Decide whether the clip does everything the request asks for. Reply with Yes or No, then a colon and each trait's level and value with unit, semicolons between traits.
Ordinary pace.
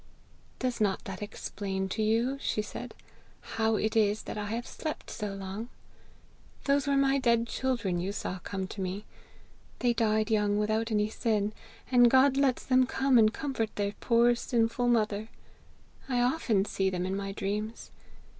Yes: average, 165 wpm